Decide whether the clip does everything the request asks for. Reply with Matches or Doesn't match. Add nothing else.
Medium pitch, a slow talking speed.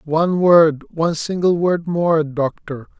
Matches